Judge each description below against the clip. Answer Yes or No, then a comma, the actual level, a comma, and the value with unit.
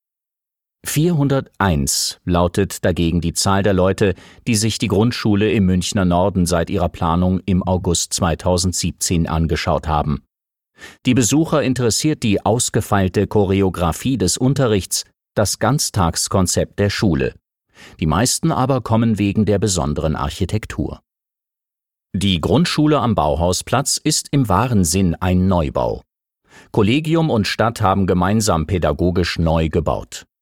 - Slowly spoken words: Yes, slow, 120 wpm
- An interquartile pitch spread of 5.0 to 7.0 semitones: No, average, 4.4 semitones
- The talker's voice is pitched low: Yes, very low, 95 Hz